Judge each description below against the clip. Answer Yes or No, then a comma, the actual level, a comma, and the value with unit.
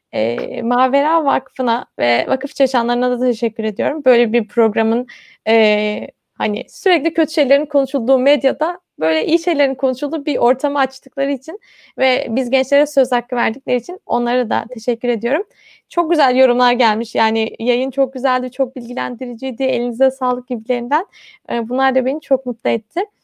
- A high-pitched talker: Yes, very high, 260 Hz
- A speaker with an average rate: No, fast, 145 wpm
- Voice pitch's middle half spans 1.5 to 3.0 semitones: Yes, average, 2.7 semitones